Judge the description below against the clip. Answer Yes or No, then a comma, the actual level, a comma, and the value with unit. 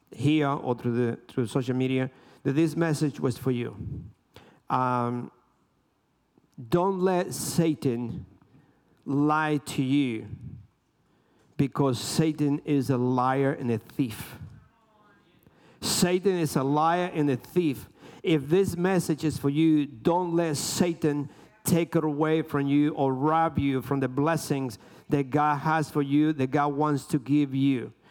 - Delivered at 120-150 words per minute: Yes, average, 140 wpm